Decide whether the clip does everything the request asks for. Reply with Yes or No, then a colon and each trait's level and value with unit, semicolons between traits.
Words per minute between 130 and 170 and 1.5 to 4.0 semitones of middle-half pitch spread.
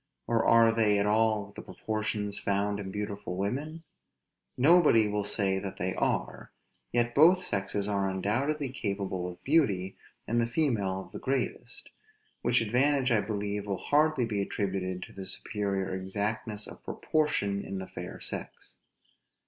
Yes: average, 150 wpm; average, 3.6 semitones